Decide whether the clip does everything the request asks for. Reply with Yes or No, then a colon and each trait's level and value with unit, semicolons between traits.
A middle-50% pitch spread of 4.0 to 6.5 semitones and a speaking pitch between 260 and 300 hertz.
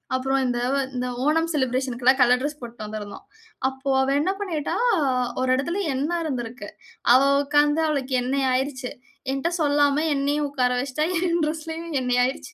No: average, 2.9 semitones; very high, 270 Hz